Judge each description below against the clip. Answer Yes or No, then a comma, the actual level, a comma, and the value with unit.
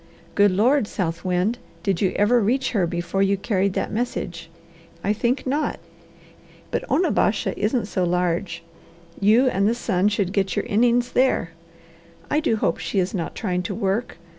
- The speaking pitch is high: Yes, high, 200 Hz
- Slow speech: No, average, 165 wpm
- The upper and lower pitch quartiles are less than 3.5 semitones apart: No, average, 4.5 semitones